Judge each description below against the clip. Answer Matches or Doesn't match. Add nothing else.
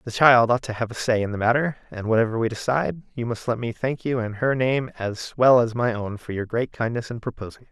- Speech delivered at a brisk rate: Matches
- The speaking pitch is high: Doesn't match